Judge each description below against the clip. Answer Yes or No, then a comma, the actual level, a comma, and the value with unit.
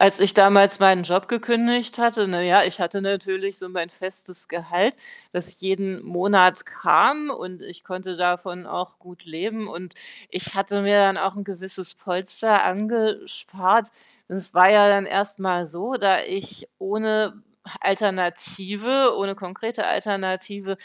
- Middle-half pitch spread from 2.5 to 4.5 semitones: No, narrow, 1.9 semitones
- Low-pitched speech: No, high, 195 Hz